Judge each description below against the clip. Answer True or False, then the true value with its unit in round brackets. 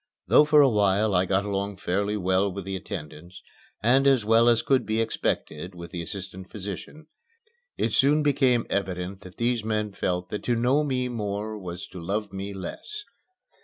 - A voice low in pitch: True (100 Hz)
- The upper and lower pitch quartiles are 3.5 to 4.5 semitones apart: True (4.2 semitones)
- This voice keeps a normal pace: True (180 wpm)